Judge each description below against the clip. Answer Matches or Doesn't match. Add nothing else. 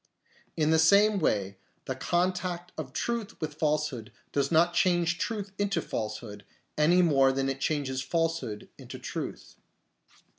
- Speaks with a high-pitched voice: Doesn't match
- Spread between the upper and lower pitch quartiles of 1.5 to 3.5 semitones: Doesn't match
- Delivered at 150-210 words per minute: Doesn't match